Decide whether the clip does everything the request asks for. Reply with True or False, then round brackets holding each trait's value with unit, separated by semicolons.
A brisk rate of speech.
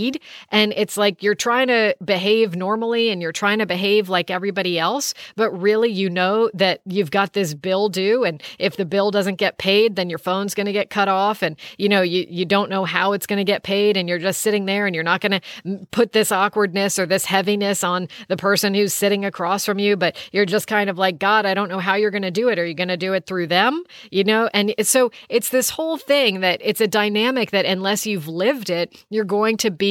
True (245 wpm)